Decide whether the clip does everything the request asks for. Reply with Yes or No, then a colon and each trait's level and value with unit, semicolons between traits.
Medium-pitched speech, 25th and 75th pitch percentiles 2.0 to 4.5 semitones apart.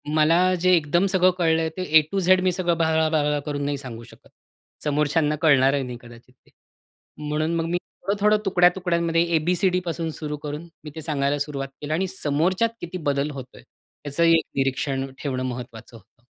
Yes: medium, 155 Hz; average, 3.6 semitones